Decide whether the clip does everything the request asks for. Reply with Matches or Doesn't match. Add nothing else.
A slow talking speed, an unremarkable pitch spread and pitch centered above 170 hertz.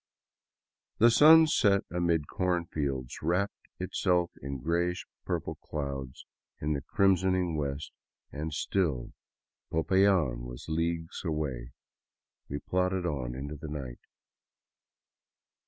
Doesn't match